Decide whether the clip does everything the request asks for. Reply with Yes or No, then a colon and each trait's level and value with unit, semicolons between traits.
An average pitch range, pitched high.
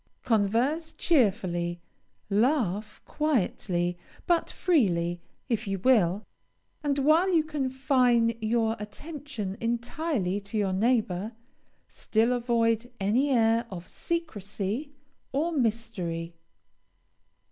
No: wide, 5.7 semitones; high, 230 Hz